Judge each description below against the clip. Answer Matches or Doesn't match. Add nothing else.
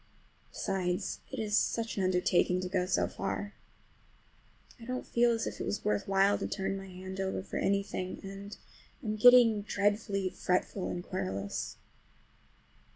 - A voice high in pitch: Matches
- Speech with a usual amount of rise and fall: Doesn't match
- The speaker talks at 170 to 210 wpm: Doesn't match